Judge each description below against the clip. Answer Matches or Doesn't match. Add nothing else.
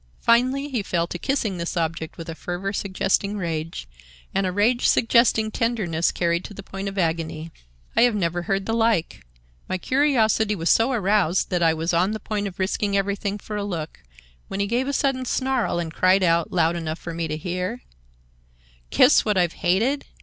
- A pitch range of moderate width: Matches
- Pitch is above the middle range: Matches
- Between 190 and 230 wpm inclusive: Matches